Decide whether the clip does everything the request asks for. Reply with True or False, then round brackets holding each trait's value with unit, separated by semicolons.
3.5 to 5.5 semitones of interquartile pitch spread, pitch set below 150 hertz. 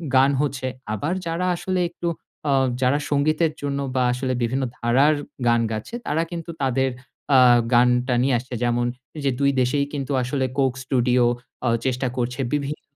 False (2.7 semitones; 135 Hz)